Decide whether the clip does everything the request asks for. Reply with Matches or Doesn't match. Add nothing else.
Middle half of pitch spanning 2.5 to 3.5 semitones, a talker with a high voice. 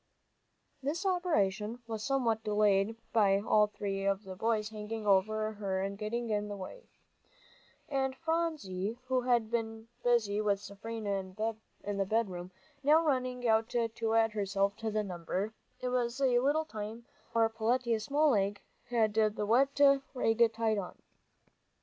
Matches